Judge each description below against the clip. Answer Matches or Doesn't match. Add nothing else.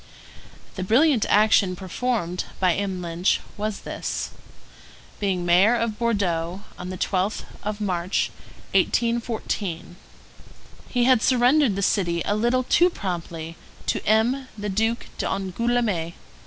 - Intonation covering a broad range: Doesn't match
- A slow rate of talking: Matches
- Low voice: Doesn't match